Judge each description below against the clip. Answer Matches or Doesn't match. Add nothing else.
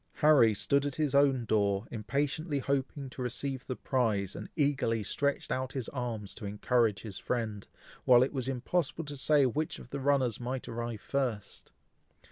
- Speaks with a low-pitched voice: Matches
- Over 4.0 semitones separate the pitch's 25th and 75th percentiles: Doesn't match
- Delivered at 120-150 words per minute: Doesn't match